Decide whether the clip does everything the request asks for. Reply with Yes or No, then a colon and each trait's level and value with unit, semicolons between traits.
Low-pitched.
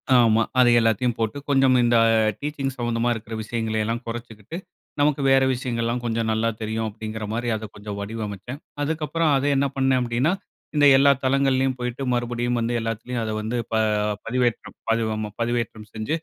Yes: low, 120 Hz